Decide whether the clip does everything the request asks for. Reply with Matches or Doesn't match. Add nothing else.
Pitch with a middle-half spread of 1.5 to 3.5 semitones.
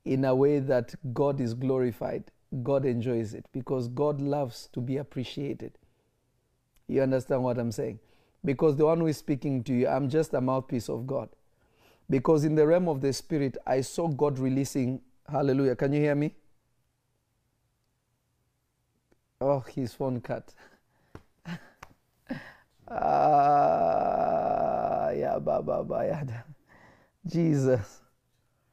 Matches